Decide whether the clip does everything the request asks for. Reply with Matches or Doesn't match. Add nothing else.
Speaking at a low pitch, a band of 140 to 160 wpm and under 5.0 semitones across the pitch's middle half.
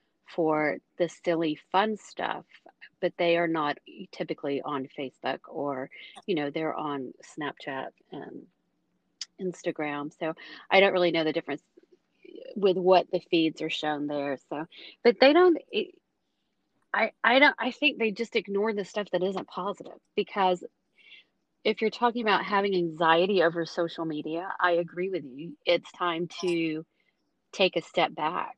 Doesn't match